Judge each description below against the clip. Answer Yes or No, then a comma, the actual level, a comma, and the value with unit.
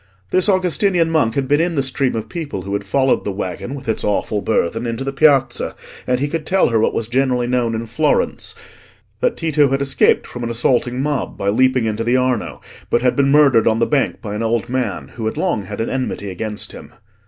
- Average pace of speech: No, fast, 220 wpm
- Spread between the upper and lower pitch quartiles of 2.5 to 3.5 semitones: No, average, 3.9 semitones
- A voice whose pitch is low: Yes, low, 125 Hz